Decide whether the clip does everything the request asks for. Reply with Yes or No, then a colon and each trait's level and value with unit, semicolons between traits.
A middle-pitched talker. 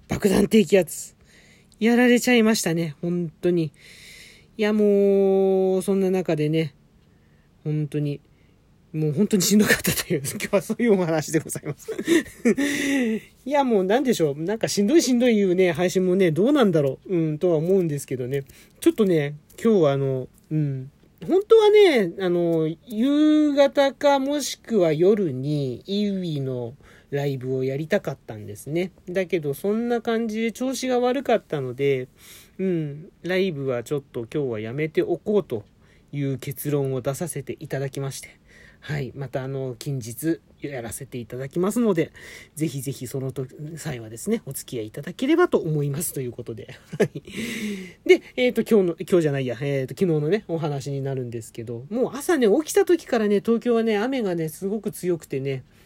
Yes: medium, 175 Hz